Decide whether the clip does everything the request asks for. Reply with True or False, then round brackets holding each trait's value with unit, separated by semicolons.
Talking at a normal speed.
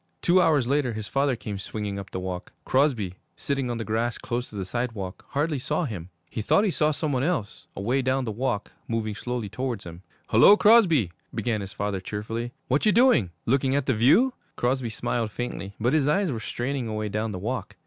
False (210 wpm)